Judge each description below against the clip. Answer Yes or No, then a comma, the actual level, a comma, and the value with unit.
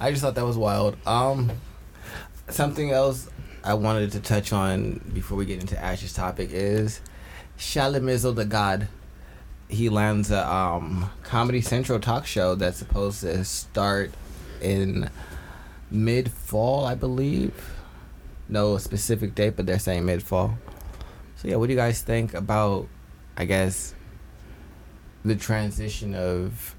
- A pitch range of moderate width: Yes, average, 3.6 semitones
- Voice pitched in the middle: No, low, 105 Hz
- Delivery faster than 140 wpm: No, slow, 135 wpm